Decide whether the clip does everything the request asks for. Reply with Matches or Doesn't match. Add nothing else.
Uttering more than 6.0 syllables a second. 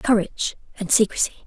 Matches